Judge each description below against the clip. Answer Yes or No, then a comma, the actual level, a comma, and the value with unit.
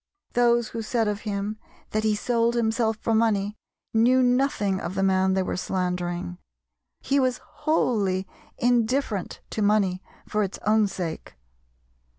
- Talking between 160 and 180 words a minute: No, average, 145 wpm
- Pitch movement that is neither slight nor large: Yes, average, 3.7 semitones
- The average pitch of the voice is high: Yes, high, 215 Hz